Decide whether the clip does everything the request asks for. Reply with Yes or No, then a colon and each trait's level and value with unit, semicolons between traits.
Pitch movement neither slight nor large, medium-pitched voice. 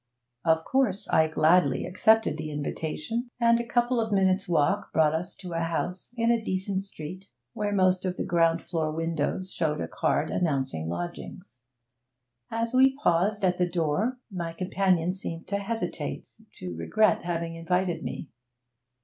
Yes: average, 3.8 semitones; medium, 180 Hz